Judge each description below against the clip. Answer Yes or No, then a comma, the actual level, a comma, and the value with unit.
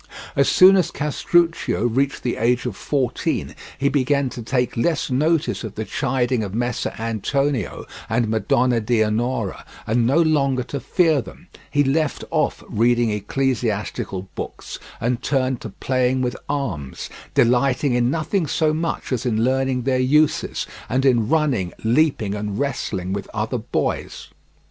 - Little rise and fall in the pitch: No, average, 3.5 semitones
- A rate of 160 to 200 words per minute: No, average, 150 wpm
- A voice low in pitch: Yes, low, 125 Hz